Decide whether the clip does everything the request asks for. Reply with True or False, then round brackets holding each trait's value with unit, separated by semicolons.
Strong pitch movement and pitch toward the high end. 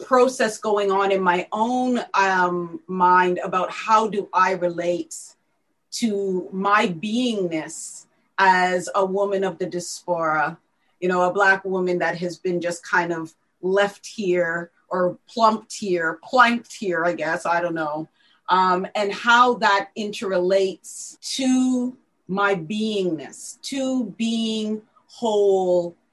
False (3.5 semitones; 195 Hz)